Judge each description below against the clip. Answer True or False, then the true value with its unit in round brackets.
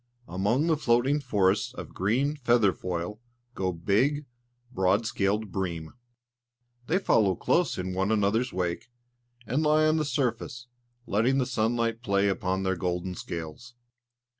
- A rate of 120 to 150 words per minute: True (140 wpm)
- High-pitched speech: False (110 Hz)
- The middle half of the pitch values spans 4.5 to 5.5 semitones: True (5.1 semitones)